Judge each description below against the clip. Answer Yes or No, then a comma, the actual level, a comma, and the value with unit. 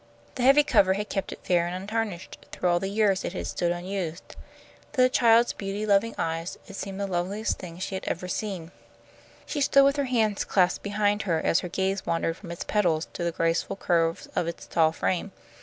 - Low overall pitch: No, high, 190 Hz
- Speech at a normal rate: No, fast, 210 wpm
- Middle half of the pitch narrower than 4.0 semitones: Yes, average, 3.3 semitones